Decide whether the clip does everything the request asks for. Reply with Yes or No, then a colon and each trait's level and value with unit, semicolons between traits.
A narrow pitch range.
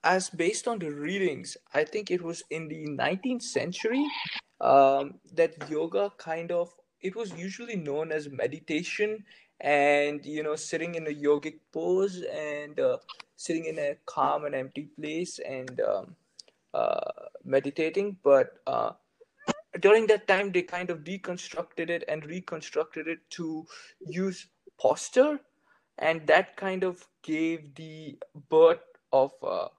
No: average, 4.1 semitones